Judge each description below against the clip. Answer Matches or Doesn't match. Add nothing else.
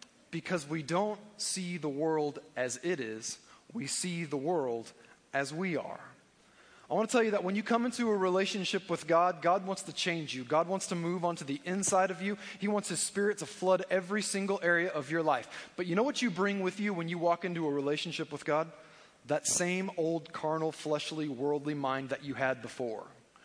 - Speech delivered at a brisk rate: Matches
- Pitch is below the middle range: Doesn't match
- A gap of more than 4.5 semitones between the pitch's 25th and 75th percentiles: Doesn't match